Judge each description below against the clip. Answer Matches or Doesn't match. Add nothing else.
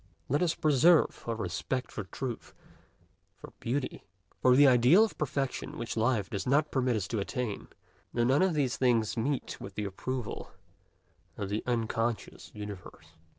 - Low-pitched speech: Matches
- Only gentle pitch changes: Doesn't match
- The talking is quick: Doesn't match